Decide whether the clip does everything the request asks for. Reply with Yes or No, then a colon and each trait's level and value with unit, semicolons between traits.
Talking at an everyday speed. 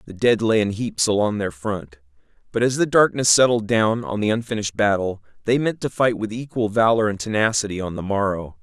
No: fast, 210 wpm